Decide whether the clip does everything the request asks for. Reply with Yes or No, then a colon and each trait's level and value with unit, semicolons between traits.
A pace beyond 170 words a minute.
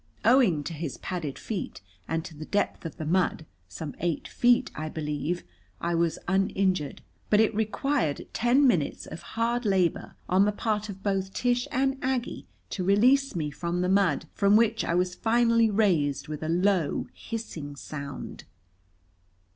No: average, 165 wpm